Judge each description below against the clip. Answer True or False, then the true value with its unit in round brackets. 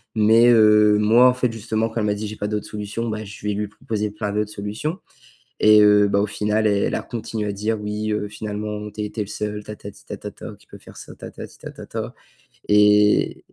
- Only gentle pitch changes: True (0.8 semitones)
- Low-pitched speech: True (105 Hz)